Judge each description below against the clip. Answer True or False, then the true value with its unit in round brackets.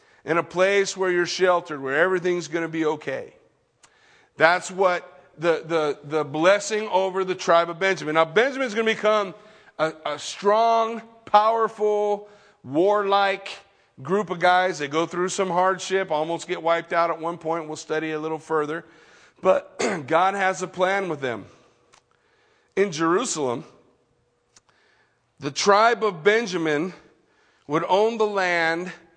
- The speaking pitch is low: False (180 Hz)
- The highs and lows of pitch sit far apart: False (3.7 semitones)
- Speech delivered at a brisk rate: False (140 wpm)